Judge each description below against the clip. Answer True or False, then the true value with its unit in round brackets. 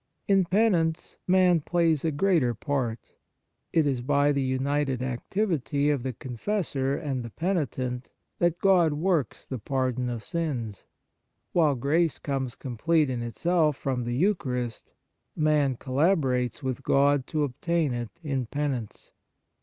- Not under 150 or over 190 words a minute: False (140 wpm)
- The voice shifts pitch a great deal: False (4.6 semitones)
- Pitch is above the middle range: False (140 Hz)